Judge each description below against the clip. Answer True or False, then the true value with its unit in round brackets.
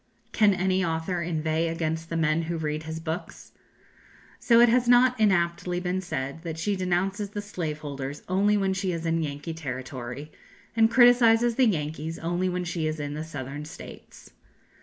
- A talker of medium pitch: True (170 Hz)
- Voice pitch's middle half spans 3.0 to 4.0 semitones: True (3.7 semitones)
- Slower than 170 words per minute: False (175 wpm)